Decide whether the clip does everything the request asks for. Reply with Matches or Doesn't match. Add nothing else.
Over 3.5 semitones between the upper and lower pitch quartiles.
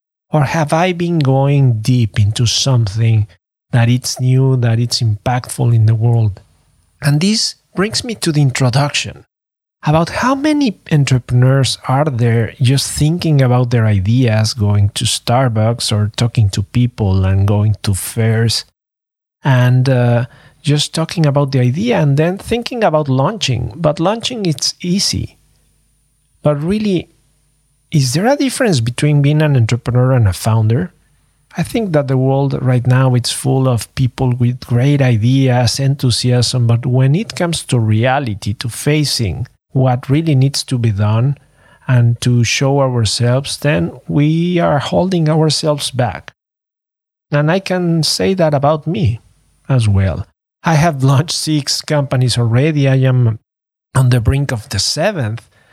Matches